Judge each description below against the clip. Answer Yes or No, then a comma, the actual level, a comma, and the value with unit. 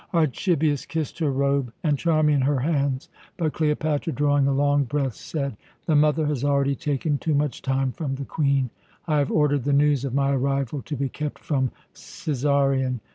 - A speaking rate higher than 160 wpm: Yes, average, 180 wpm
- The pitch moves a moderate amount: No, narrow, 1.7 semitones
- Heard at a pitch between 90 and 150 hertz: Yes, medium, 140 Hz